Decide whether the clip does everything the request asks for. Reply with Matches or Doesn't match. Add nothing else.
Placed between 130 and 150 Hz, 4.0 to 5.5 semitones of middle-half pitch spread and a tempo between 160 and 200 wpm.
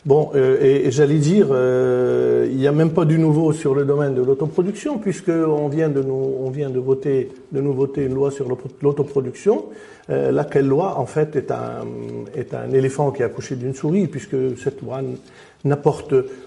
Doesn't match